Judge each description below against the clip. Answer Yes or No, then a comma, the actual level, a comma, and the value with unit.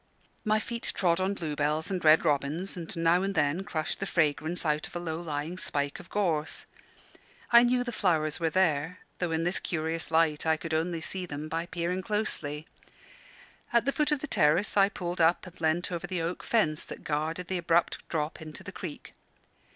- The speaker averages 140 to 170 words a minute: No, average, 195 wpm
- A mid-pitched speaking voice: Yes, medium, 170 Hz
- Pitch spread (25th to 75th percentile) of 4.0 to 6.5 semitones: No, average, 3.0 semitones